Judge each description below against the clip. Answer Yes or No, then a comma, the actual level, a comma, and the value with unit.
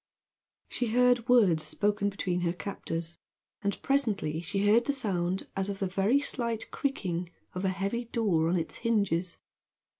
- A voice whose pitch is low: No, high, 200 Hz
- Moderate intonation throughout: Yes, average, 4.7 semitones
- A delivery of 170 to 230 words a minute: No, average, 155 wpm